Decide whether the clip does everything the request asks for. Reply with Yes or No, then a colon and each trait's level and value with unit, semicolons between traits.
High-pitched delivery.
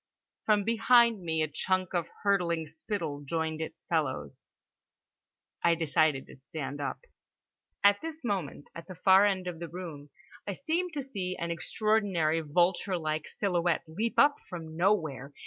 No: medium, 175 Hz